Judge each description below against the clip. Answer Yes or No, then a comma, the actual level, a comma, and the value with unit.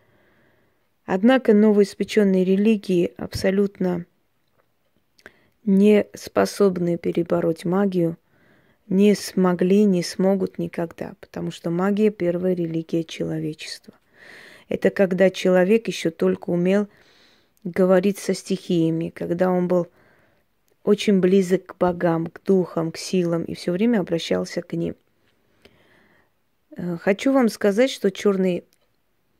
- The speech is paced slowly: Yes, slow, 100 wpm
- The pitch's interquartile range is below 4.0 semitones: Yes, narrow, 2.5 semitones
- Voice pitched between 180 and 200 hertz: Yes, medium, 185 Hz